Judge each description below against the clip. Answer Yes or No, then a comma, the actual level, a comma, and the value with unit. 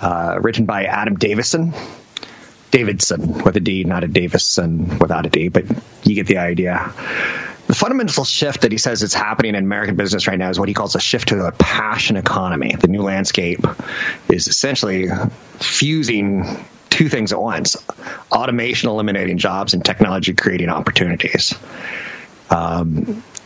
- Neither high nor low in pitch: No, low, 105 Hz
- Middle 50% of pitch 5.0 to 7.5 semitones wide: Yes, average, 5.3 semitones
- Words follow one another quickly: No, average, 155 wpm